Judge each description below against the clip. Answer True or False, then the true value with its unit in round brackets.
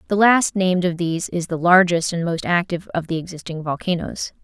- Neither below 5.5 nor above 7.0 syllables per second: True (5.8 syllables/s)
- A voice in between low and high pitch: True (175 Hz)